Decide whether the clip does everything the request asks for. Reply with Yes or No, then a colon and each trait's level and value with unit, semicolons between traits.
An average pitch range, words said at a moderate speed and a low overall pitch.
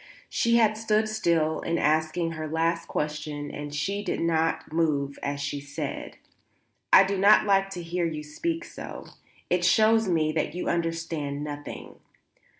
No: average, 4.3 semitones; average, 160 wpm; medium, 165 Hz